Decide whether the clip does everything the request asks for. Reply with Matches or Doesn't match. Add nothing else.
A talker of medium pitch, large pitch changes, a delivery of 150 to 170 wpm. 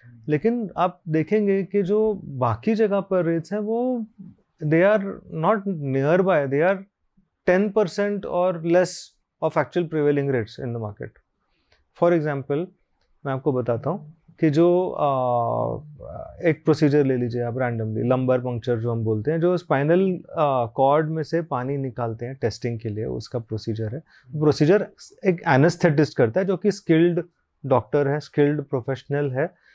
Matches